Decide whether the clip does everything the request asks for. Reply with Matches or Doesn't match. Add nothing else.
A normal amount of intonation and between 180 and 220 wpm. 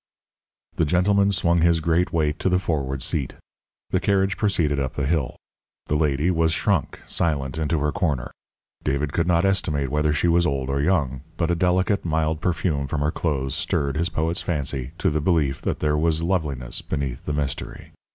Matches